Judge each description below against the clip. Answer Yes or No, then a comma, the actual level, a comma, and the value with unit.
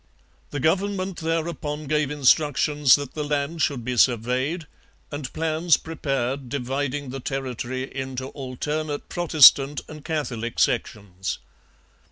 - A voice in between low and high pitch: Yes, medium, 145 Hz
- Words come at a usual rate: No, slow, 115 wpm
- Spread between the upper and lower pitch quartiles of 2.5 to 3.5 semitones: Yes, average, 3.2 semitones